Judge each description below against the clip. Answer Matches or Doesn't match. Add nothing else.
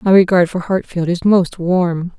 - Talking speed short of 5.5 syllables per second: Matches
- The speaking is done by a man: Doesn't match